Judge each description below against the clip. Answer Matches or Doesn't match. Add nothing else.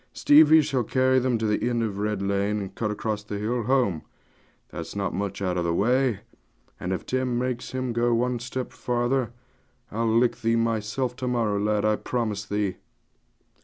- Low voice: Matches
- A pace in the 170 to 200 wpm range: Matches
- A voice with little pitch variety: Doesn't match